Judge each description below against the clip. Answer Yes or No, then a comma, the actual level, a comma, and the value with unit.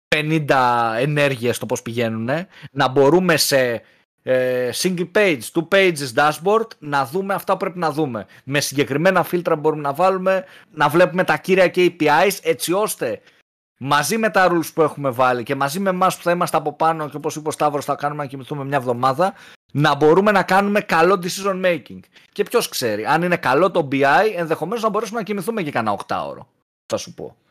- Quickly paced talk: Yes, fast, 195 wpm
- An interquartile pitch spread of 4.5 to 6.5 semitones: Yes, average, 5.1 semitones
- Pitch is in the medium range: Yes, medium, 160 Hz